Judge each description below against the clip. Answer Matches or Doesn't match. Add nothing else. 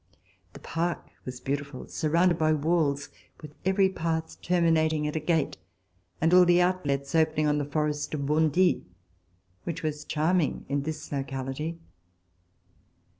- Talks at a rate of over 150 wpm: Doesn't match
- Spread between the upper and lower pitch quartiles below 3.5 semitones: Matches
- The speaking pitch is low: Doesn't match